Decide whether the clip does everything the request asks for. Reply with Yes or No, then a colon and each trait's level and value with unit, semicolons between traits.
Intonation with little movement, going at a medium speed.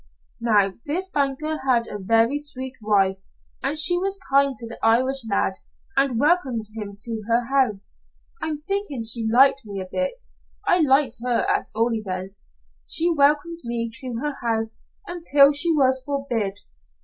No: average, 4.5 semitones; average, 160 wpm